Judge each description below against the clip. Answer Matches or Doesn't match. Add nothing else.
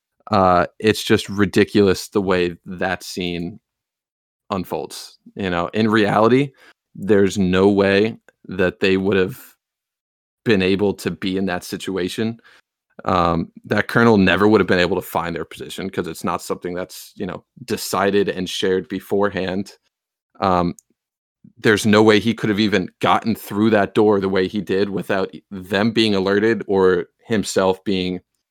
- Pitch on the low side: Matches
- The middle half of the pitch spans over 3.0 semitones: Doesn't match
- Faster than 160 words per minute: Doesn't match